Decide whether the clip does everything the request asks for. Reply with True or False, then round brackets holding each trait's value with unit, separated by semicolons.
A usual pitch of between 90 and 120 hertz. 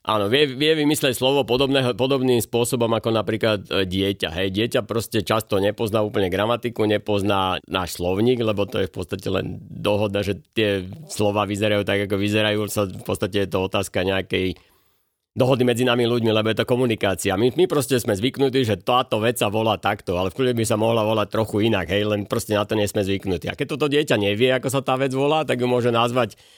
True (110 Hz)